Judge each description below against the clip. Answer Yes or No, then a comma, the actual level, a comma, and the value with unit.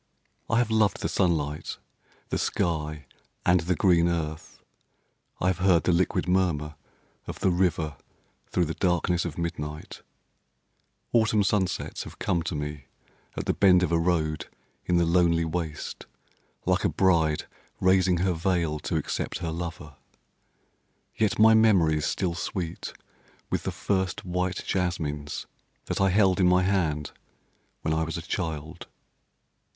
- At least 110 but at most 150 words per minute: Yes, average, 145 wpm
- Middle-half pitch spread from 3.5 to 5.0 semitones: No, average, 2.7 semitones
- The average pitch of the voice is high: No, very low, 85 Hz